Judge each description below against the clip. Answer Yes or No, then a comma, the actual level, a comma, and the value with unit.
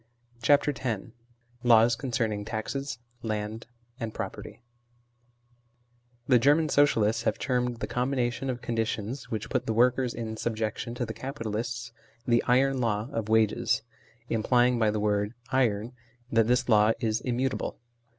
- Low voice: Yes, low, 115 Hz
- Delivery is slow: No, average, 145 wpm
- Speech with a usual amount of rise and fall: No, narrow, 2.2 semitones